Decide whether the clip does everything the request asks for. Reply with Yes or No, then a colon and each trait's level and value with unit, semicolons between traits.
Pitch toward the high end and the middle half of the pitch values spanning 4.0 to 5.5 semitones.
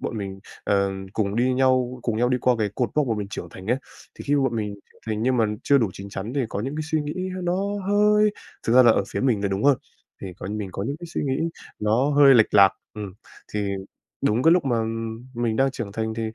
No: low, 120 Hz; average, 4.3 semitones